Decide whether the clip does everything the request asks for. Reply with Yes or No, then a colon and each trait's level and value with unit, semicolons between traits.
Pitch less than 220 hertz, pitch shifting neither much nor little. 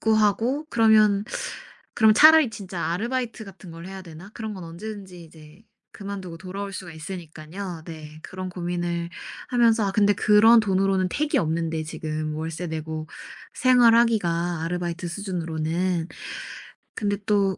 Yes: medium, 185 Hz; average, 4.2 semitones